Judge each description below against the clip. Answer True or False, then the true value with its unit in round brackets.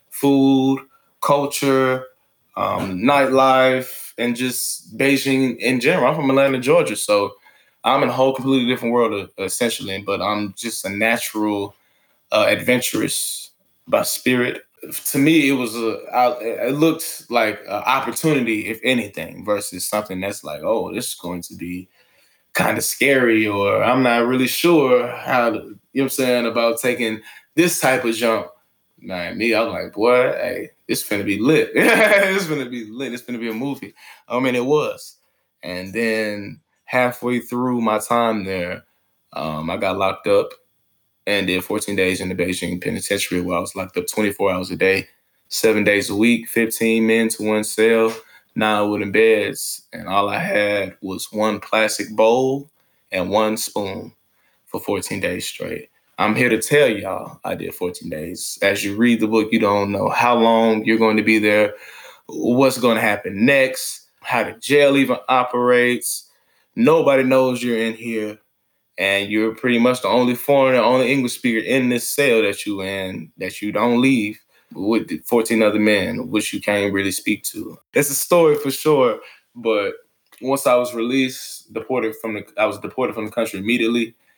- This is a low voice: True (120 Hz)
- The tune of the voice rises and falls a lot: False (3.7 semitones)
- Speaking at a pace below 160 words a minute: False (175 wpm)